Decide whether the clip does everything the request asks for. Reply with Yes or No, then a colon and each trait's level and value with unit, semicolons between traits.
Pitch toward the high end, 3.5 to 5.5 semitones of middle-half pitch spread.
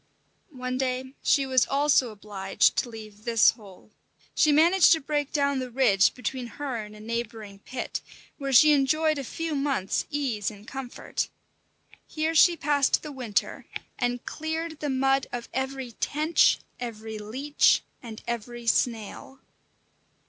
Yes: very high, 260 Hz; average, 4.3 semitones